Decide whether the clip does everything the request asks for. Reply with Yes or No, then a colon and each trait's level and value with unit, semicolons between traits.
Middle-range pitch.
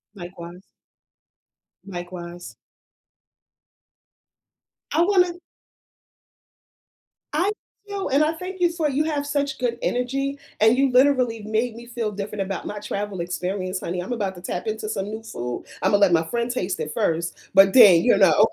No: high, 220 Hz